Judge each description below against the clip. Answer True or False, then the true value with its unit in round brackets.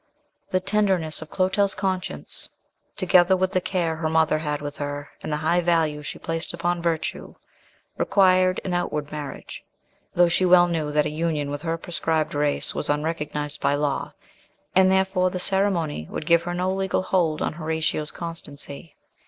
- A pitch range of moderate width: True (3.3 semitones)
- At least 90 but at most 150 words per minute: False (170 wpm)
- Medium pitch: True (165 Hz)